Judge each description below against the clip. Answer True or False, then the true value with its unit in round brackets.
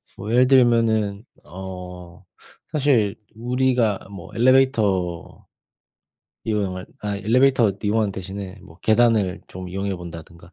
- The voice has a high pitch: False (105 Hz)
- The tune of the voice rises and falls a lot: False (4.2 semitones)